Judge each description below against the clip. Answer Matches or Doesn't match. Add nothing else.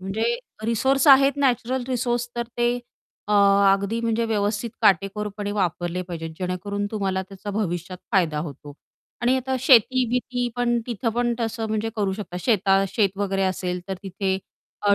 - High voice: Matches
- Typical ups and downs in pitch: Matches